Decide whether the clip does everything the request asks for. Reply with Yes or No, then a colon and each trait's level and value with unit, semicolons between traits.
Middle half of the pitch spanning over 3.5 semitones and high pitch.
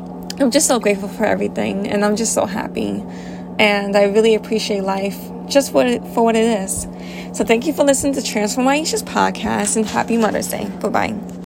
No: average, 2.7 semitones; high, 215 Hz